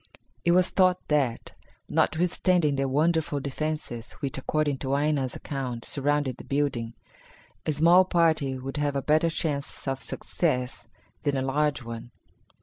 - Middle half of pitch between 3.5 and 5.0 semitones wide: No, average, 2.9 semitones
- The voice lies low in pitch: No, medium, 145 Hz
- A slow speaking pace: No, average, 145 wpm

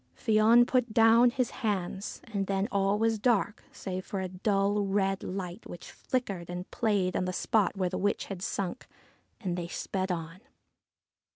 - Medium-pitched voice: No, high, 195 Hz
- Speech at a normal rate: Yes, average, 170 wpm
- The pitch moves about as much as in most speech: Yes, average, 3.2 semitones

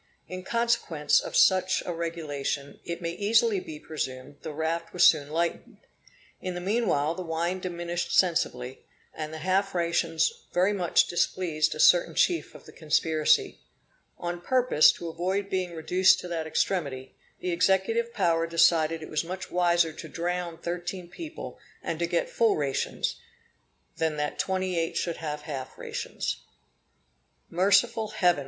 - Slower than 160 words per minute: Yes, average, 150 wpm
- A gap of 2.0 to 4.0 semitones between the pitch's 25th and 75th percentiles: Yes, average, 2.8 semitones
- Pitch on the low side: No, medium, 170 Hz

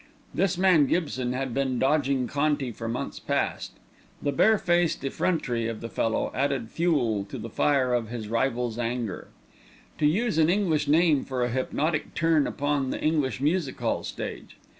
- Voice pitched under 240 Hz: Yes, medium, 140 Hz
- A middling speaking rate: Yes, average, 160 wpm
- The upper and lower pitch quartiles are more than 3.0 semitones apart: Yes, average, 4.4 semitones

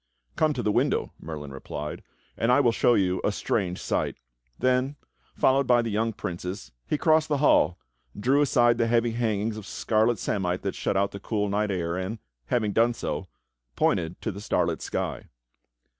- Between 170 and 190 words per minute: Yes, average, 180 wpm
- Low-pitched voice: Yes, low, 110 Hz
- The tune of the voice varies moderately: Yes, average, 4.0 semitones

